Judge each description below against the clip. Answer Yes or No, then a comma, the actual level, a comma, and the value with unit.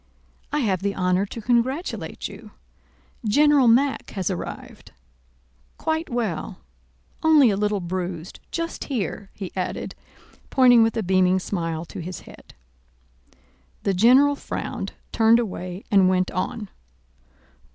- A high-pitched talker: Yes, high, 205 Hz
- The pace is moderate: No, slow, 125 wpm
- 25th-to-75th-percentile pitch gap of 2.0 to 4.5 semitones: No, average, 5.2 semitones